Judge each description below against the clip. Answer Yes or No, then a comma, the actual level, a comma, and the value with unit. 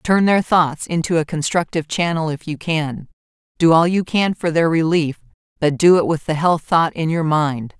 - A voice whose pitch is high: No, medium, 160 Hz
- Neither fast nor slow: No, fast, 210 wpm